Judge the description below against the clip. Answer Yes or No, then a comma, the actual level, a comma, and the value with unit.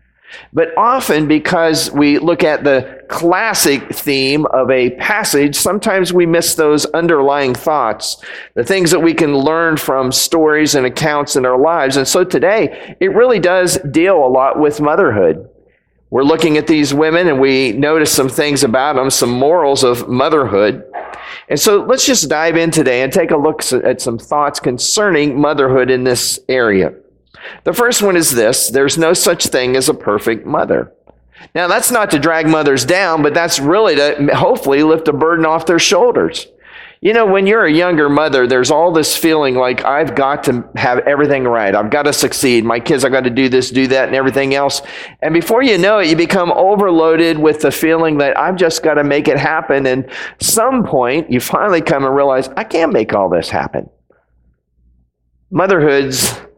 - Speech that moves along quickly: No, average, 185 wpm